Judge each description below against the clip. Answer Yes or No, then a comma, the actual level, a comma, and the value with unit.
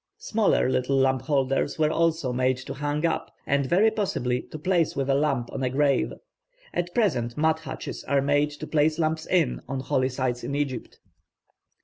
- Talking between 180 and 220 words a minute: Yes, average, 185 wpm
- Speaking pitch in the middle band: Yes, medium, 145 Hz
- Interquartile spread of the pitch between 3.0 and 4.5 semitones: Yes, average, 3.4 semitones